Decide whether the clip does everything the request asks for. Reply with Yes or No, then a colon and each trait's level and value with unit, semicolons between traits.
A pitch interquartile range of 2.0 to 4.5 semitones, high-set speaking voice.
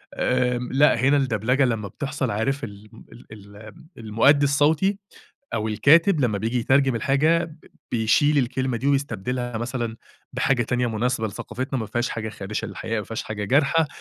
No: average, 4.1 semitones; low, 125 Hz